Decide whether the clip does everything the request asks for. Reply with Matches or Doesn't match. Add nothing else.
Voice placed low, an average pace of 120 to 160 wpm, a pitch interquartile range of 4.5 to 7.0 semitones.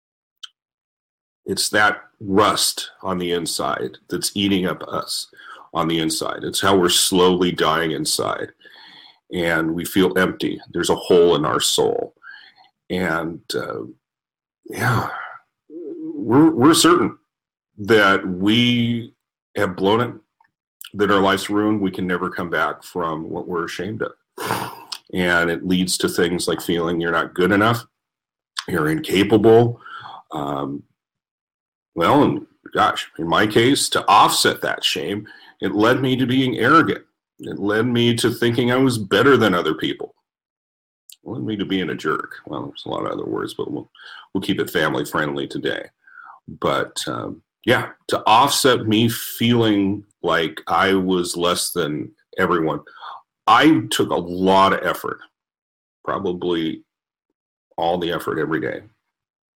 Matches